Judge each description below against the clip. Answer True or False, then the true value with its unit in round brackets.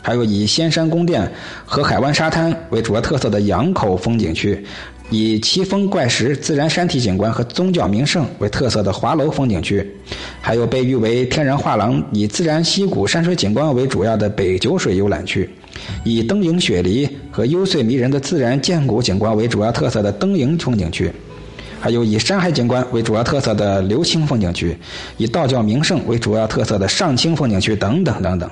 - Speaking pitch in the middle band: False (115 Hz)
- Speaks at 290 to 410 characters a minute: True (300 characters per minute)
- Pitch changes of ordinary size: False (7.0 semitones)